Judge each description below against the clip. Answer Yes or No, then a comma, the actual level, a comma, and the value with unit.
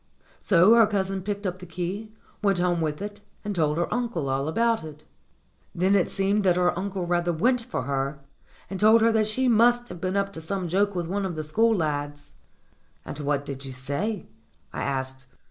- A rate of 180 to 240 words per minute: Yes, fast, 205 wpm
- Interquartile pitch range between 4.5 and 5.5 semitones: Yes, average, 5.0 semitones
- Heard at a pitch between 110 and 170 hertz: No, medium, 185 Hz